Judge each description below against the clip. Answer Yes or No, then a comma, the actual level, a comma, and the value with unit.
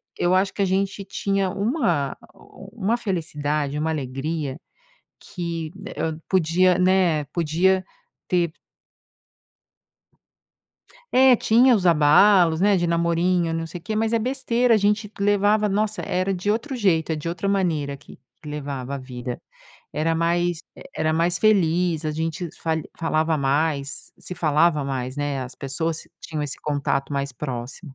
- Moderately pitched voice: Yes, medium, 170 Hz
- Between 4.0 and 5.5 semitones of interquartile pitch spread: Yes, average, 4.5 semitones